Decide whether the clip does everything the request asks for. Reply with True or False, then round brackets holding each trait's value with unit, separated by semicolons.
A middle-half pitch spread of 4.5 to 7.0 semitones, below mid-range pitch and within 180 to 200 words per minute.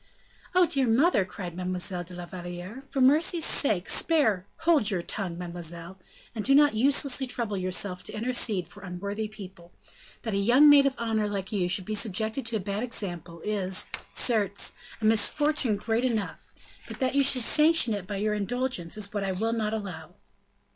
False (5.2 semitones; 210 Hz; 185 wpm)